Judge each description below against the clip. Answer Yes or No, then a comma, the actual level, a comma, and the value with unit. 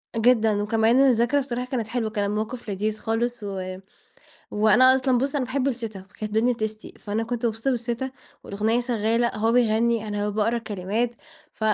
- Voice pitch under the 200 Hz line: No, high, 225 Hz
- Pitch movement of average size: No, narrow, 2.3 semitones